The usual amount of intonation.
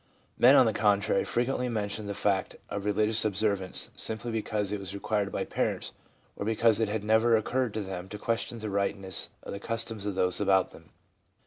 No: narrow, 2.1 semitones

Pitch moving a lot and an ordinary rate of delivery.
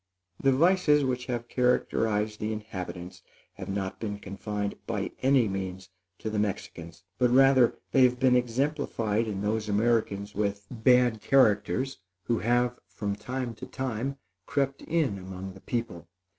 No: average, 3.9 semitones; average, 145 wpm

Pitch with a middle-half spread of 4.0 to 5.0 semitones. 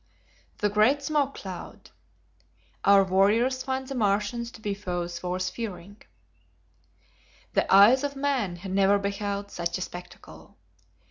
Yes: average, 4.6 semitones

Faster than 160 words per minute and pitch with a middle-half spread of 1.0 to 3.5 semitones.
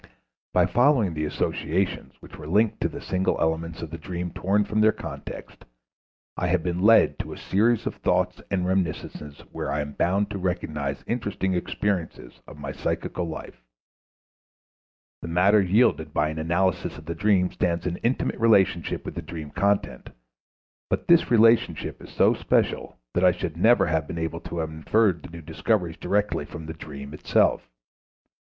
No: average, 175 wpm; average, 4.0 semitones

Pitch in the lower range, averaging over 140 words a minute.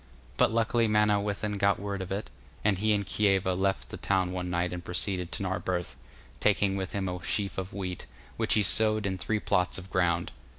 Yes: very low, 95 Hz; average, 200 wpm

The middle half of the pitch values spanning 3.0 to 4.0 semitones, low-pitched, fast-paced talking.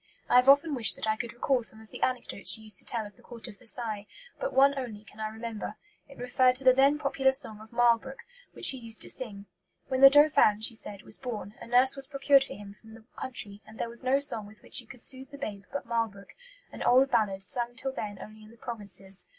No: average, 3.6 semitones; high, 235 Hz; fast, 250 wpm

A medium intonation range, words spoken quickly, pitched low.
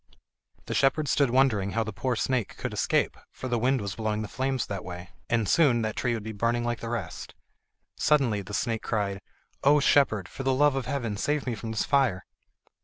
Yes: average, 4.0 semitones; fast, 210 wpm; low, 115 Hz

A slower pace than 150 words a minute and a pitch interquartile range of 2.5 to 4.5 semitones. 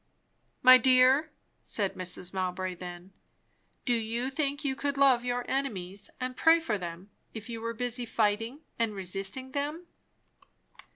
No: average, 140 wpm; average, 5.3 semitones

